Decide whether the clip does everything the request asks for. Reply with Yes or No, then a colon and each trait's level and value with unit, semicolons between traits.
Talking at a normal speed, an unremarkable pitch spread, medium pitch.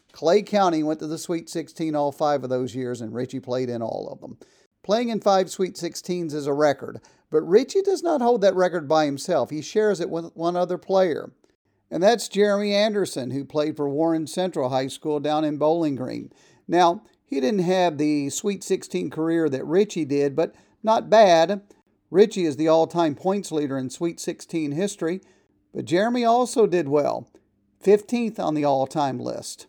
Yes: average, 190 wpm; average, 4.6 semitones; medium, 165 Hz